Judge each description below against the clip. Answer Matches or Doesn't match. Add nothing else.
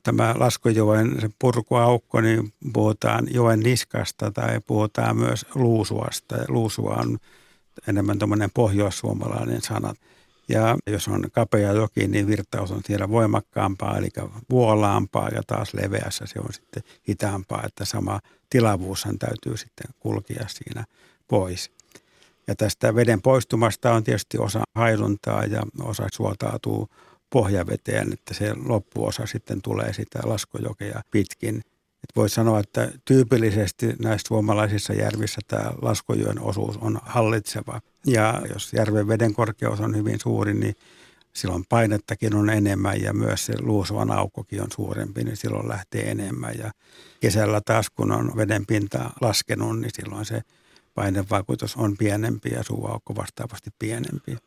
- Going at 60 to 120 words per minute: Doesn't match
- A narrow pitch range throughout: Matches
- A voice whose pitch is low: Matches